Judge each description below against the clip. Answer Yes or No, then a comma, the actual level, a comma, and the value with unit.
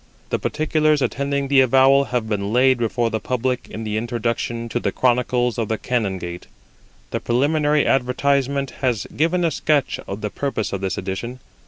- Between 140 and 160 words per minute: No, average, 170 wpm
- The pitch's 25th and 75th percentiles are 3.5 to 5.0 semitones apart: Yes, average, 3.8 semitones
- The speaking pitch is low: Yes, low, 125 Hz